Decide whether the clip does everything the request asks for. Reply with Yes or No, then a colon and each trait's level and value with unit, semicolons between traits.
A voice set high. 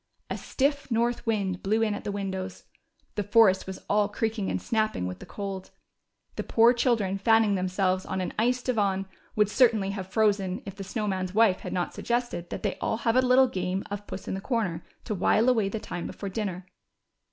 Yes: high, 205 Hz